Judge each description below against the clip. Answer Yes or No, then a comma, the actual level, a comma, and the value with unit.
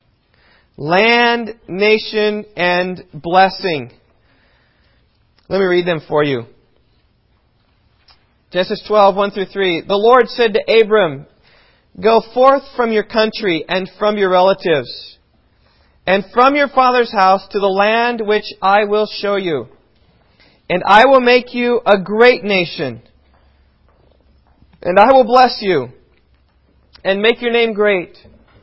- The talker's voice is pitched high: Yes, high, 200 Hz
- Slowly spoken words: Yes, slow, 125 wpm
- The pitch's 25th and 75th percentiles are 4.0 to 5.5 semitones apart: Yes, average, 5.1 semitones